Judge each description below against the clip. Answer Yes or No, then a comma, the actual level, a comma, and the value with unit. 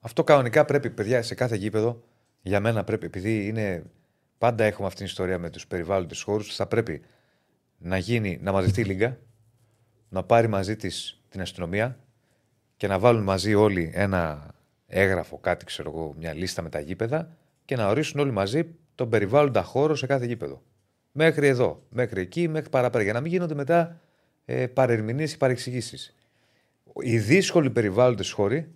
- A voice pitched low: Yes, low, 115 Hz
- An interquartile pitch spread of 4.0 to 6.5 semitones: Yes, wide, 5.4 semitones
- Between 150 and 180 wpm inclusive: Yes, average, 165 wpm